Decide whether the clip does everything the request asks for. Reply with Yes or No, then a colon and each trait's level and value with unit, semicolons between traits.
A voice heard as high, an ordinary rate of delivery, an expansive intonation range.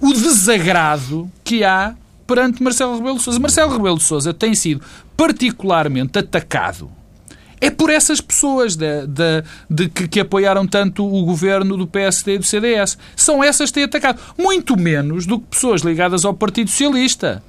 Yes: high, 200 Hz; average, 170 wpm; wide, 6.2 semitones